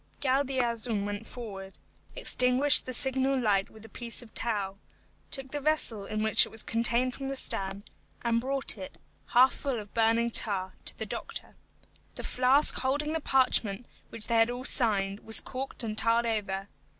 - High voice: Yes, high, 235 Hz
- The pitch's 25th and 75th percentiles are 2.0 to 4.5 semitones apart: Yes, average, 3.5 semitones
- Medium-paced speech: Yes, average, 175 wpm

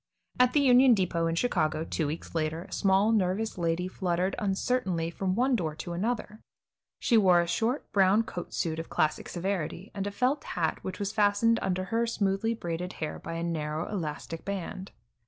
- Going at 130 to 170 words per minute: No, average, 185 wpm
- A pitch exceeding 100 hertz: Yes, high, 190 Hz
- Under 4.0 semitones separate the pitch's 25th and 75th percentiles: No, average, 4.6 semitones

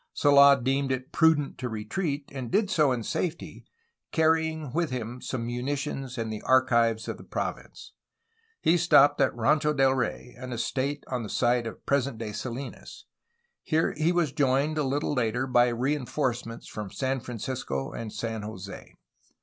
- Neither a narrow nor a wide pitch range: Yes, average, 3.6 semitones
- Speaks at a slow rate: No, average, 165 wpm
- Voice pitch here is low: Yes, low, 130 Hz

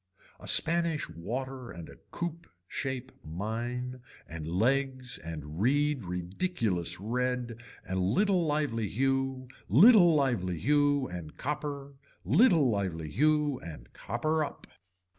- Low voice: Yes, low, 125 Hz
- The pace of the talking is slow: Yes, slow, 115 wpm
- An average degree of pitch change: No, wide, 7.8 semitones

